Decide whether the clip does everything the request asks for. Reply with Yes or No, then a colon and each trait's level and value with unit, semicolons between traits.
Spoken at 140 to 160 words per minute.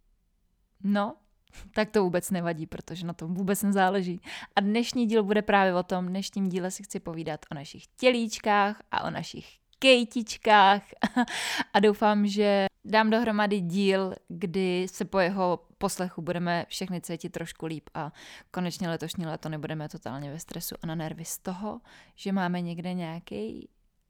Yes: average, 155 wpm